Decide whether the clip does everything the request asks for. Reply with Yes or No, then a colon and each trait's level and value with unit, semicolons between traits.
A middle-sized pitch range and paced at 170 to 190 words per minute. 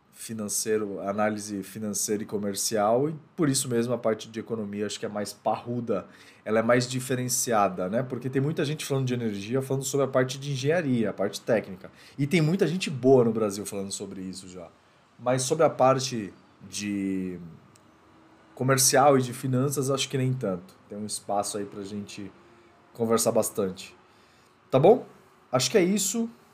Yes: average, 4.8 semitones; average, 175 wpm